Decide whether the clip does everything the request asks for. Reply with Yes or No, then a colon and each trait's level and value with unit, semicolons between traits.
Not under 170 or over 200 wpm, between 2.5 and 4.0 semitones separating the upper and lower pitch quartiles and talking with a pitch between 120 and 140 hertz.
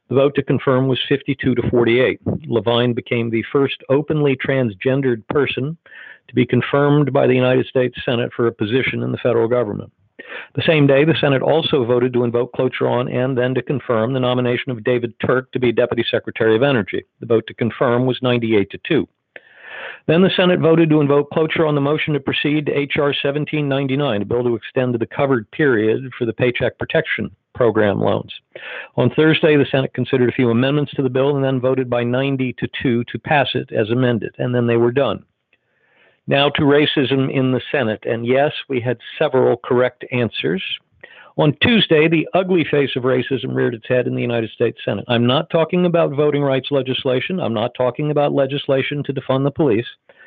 Yes: average, 195 wpm; average, 2.8 semitones; low, 130 Hz